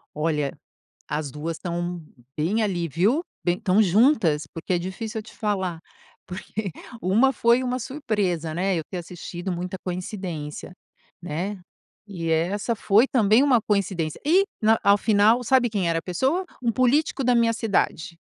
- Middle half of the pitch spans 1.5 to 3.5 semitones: No, average, 4.9 semitones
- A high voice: Yes, high, 195 Hz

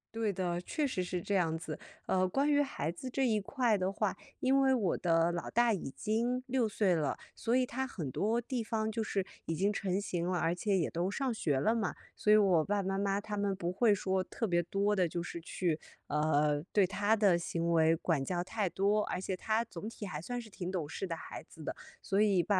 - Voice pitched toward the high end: Yes, high, 195 Hz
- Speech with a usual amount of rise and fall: Yes, average, 4.1 semitones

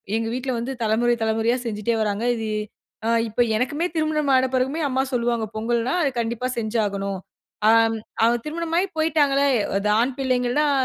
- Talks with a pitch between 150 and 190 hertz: No, high, 240 Hz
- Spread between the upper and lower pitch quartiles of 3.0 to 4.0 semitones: Yes, average, 3.4 semitones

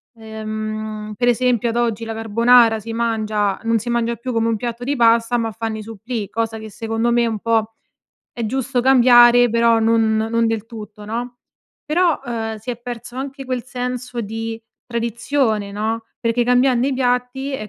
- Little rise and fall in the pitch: Yes, narrow, 1.7 semitones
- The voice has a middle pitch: No, high, 230 Hz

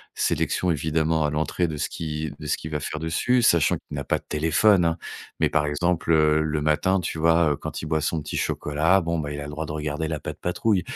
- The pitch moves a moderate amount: No, narrow, 1.8 semitones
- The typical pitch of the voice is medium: No, very low, 80 Hz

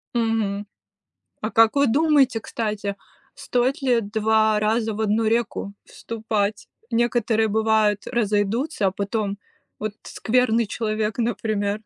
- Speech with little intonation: Yes, narrow, 2.0 semitones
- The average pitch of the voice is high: Yes, high, 220 Hz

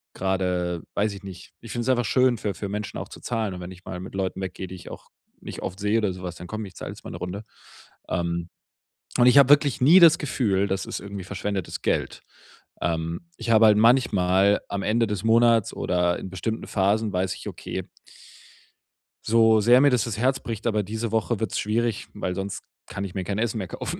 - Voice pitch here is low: Yes, low, 105 Hz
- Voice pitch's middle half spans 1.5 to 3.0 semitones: No, average, 3.5 semitones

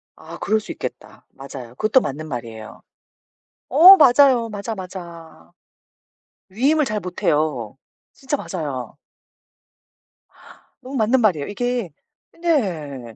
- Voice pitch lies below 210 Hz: Yes, high, 190 Hz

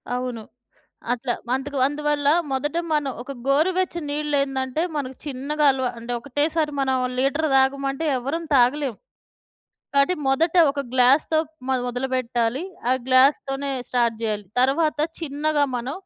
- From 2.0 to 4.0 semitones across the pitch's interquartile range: Yes, narrow, 2.6 semitones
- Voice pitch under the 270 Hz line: No, very high, 275 Hz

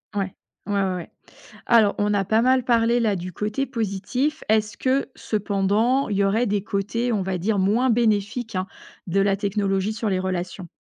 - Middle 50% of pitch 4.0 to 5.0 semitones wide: No, average, 2.9 semitones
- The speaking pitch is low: No, high, 205 Hz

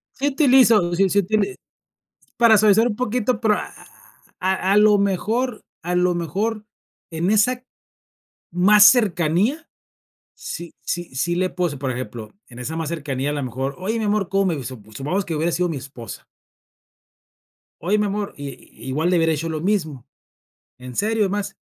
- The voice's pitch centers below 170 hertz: No, medium, 185 Hz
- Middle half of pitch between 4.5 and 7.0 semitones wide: Yes, average, 5.3 semitones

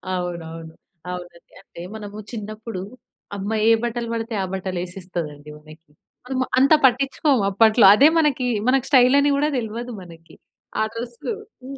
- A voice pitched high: Yes, high, 220 Hz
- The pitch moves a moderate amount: No, wide, 6.1 semitones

